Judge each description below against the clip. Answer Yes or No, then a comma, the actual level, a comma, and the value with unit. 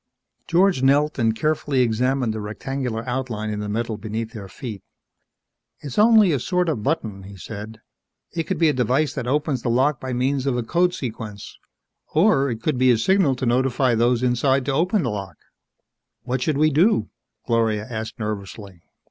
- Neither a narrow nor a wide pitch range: Yes, average, 4.6 semitones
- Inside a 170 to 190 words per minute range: Yes, average, 180 wpm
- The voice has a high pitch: No, low, 125 Hz